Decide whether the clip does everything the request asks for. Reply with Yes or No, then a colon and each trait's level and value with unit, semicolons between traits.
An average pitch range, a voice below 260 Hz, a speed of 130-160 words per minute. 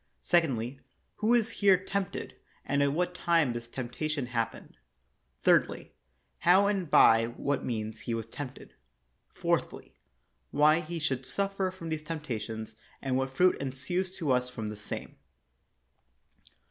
No: wide, 6.7 semitones; medium, 140 Hz; slow, 135 wpm